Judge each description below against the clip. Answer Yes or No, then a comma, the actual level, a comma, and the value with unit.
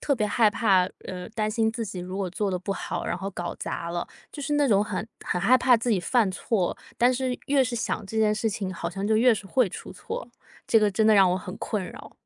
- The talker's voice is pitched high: Yes, high, 210 Hz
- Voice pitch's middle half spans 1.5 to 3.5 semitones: No, average, 3.9 semitones